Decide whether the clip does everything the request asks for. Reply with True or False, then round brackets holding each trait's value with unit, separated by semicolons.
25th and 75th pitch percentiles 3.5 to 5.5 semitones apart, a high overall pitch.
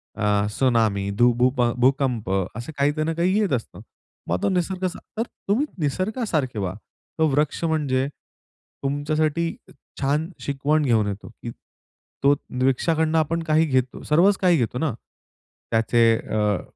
False (5.2 semitones; 140 Hz)